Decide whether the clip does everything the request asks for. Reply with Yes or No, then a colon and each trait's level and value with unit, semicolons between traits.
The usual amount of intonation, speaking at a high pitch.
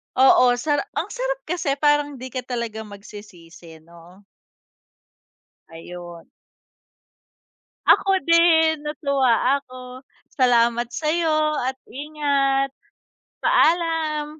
Yes: average, 4.7 semitones; very high, 275 Hz